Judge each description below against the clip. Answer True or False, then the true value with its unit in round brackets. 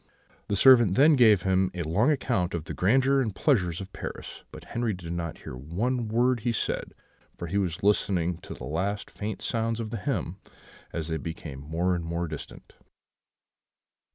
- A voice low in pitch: True (95 Hz)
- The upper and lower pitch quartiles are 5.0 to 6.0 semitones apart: True (5.4 semitones)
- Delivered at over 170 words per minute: True (180 wpm)